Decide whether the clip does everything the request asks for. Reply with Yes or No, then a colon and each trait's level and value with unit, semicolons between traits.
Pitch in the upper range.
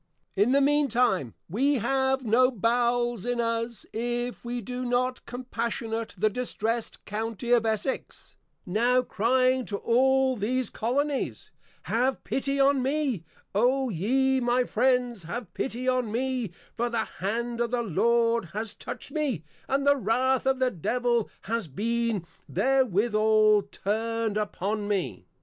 Yes: high, 240 Hz